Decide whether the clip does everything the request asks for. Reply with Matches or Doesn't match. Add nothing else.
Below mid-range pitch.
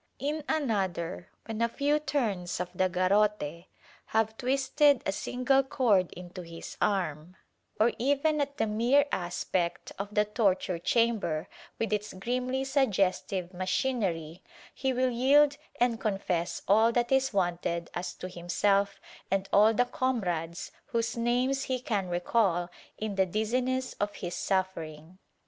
Doesn't match